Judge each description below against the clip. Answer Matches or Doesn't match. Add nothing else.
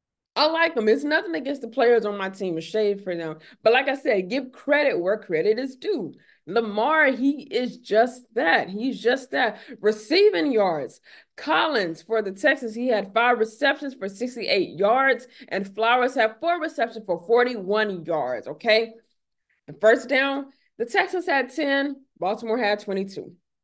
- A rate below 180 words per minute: Matches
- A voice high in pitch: Matches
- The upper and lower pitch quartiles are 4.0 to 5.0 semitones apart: Matches